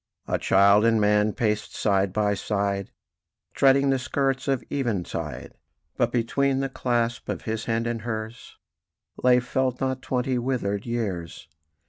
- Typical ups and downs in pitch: Yes, average, 3.9 semitones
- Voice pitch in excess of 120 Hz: No, low, 115 Hz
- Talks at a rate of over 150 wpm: No, average, 140 wpm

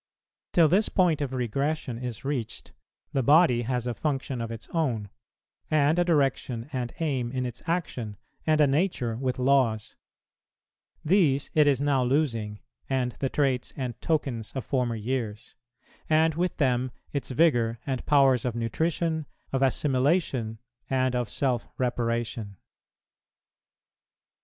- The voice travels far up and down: No, average, 3.8 semitones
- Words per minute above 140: No, slow, 135 wpm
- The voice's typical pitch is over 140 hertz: No, low, 130 Hz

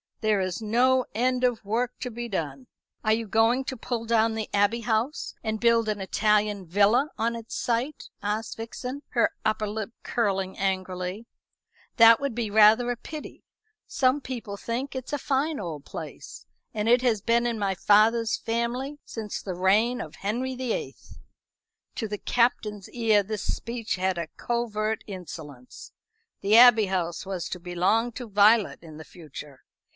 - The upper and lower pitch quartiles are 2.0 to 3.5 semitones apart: Yes, average, 3.1 semitones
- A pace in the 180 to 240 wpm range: No, average, 165 wpm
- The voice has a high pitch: Yes, high, 220 Hz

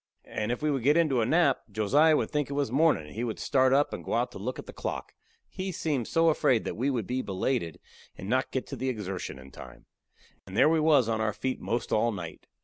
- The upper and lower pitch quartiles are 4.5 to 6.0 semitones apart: Yes, average, 5.1 semitones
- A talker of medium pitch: No, low, 130 Hz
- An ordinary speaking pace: No, fast, 250 wpm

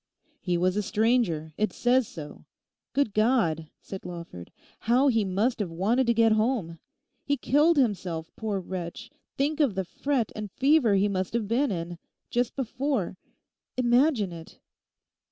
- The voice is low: No, high, 215 Hz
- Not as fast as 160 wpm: Yes, average, 150 wpm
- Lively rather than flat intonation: Yes, wide, 5.8 semitones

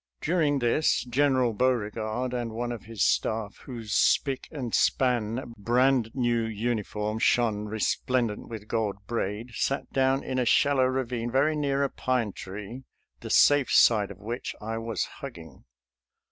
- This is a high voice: No, low, 120 Hz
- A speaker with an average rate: Yes, average, 145 wpm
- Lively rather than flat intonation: No, average, 3.1 semitones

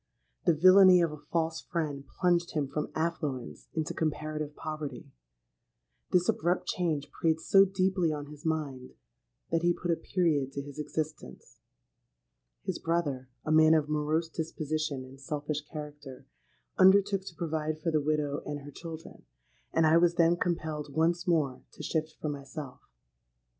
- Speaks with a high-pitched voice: No, medium, 155 Hz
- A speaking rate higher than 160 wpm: No, average, 145 wpm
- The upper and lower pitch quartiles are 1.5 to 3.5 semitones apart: Yes, narrow, 2.5 semitones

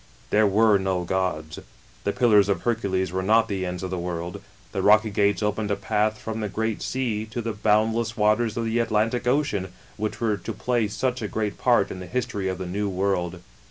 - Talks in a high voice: No, low, 105 Hz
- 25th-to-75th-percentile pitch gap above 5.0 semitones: No, average, 2.9 semitones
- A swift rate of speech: Yes, fast, 215 wpm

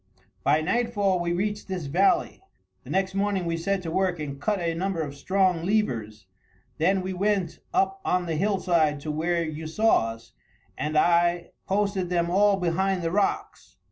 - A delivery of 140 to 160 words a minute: No, average, 170 wpm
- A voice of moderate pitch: Yes, medium, 180 Hz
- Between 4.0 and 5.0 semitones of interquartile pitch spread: No, average, 3.3 semitones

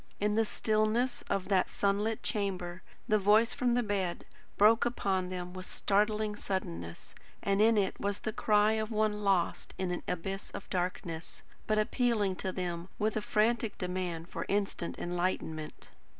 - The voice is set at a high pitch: Yes, high, 200 Hz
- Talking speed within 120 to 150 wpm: No, average, 160 wpm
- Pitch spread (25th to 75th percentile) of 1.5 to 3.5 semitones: Yes, average, 2.9 semitones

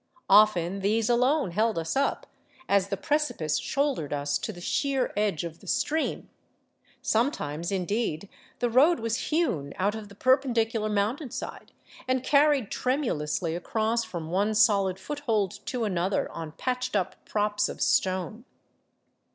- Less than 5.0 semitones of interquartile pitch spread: No, wide, 5.5 semitones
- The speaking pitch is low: No, high, 215 Hz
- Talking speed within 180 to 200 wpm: No, average, 140 wpm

